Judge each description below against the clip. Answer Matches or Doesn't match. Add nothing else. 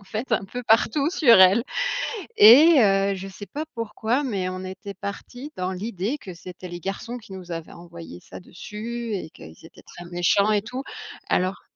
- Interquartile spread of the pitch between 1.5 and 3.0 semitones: Doesn't match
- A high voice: Matches